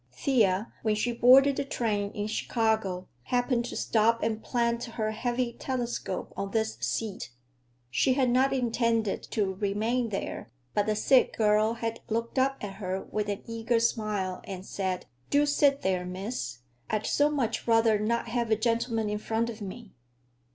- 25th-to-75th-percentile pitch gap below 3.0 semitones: Yes, narrow, 2.6 semitones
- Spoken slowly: No, average, 165 wpm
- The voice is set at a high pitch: Yes, high, 225 Hz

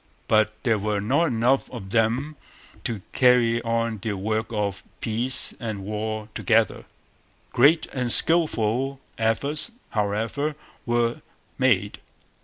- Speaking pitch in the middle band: No, low, 115 Hz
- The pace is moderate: No, slow, 115 wpm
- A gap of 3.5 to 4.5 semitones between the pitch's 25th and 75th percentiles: No, average, 2.8 semitones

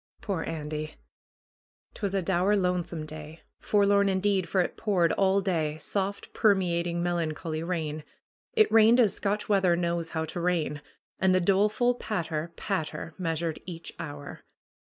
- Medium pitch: Yes, medium, 175 Hz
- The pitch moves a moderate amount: Yes, average, 3.6 semitones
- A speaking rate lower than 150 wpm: Yes, average, 140 wpm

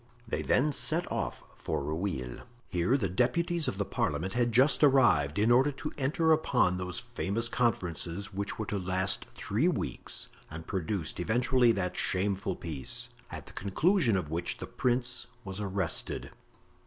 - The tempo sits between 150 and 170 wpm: Yes, average, 155 wpm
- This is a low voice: Yes, low, 100 Hz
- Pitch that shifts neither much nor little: No, wide, 5.8 semitones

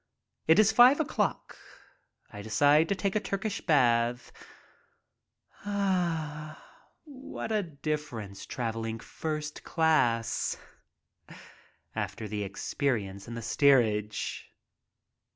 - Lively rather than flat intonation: Yes, wide, 8.0 semitones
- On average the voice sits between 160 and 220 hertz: No, medium, 145 Hz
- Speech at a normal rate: No, slow, 95 wpm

